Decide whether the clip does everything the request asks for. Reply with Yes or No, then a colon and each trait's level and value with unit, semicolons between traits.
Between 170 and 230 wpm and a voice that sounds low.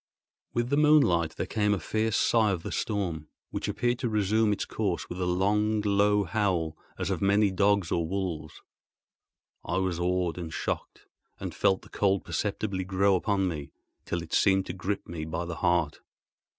Yes: average, 180 wpm; very low, 95 Hz